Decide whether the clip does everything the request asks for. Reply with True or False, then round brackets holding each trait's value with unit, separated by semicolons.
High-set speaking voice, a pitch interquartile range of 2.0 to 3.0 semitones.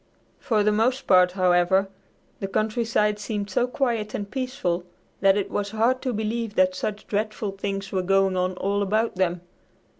True (205 Hz; 2.5 semitones)